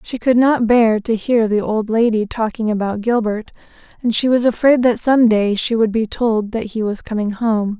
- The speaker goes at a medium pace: No, fast, 215 wpm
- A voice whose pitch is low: No, high, 225 Hz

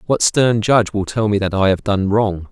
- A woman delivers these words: No, male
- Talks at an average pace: No, fast, 260 wpm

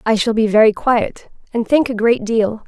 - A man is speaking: No, female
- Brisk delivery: Yes, fast, 225 wpm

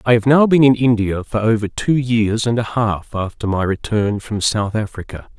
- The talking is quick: Yes, fast, 210 wpm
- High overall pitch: No, low, 110 Hz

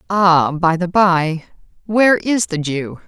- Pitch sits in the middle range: Yes, medium, 180 Hz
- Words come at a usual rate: Yes, average, 155 wpm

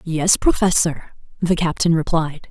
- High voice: No, medium, 170 Hz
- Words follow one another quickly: No, slow, 120 wpm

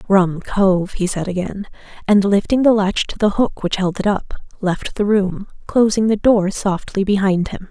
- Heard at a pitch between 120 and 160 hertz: No, high, 195 Hz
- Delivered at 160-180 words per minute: No, average, 195 wpm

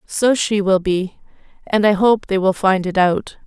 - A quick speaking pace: Yes, fast, 210 wpm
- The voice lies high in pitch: Yes, high, 195 Hz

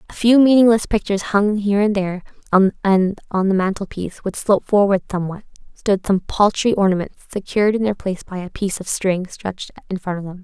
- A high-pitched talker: Yes, high, 200 Hz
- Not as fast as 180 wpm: No, average, 200 wpm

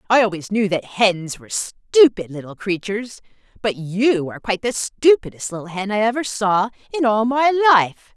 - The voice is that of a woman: Yes, female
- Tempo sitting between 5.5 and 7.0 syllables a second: No, 5.1 syllables/s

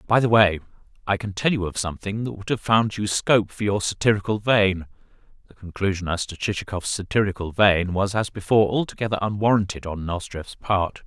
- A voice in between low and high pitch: No, low, 100 Hz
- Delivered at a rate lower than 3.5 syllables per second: Yes, 2.9 syllables/s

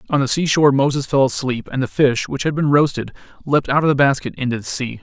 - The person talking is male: Yes, male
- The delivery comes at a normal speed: No, fast, 250 wpm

